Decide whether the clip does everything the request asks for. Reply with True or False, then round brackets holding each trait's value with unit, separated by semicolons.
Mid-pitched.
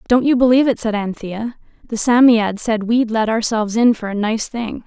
False (225 Hz)